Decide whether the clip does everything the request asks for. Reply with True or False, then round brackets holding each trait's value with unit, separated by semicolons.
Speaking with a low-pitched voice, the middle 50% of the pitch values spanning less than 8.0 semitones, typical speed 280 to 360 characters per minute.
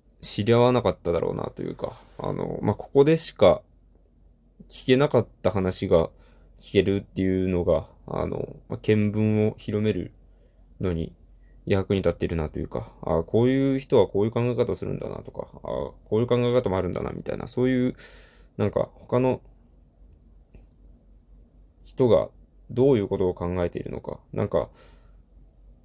True (105 Hz; 5.4 semitones; 315 characters per minute)